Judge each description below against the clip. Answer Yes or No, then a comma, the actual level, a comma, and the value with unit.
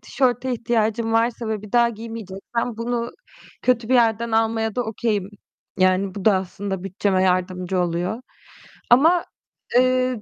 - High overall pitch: Yes, high, 225 Hz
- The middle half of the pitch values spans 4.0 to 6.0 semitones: No, average, 3.6 semitones